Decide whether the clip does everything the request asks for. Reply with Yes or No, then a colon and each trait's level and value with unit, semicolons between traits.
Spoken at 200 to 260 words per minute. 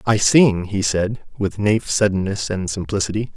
No: average, 160 wpm